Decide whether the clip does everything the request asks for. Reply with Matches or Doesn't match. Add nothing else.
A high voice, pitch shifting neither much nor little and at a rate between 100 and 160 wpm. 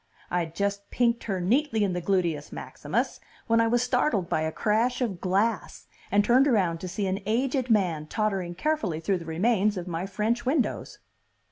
Doesn't match